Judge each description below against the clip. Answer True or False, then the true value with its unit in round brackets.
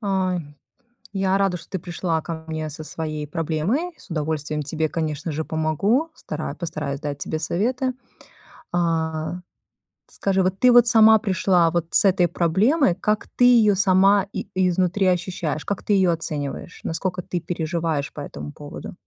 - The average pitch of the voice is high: False (175 Hz)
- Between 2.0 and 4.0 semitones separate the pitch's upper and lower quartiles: True (3.7 semitones)